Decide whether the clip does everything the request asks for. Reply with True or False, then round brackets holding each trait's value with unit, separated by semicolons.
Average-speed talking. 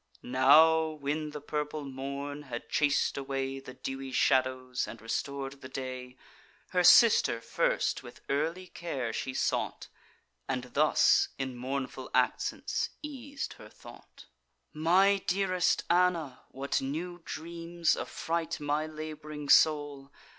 False (120 wpm)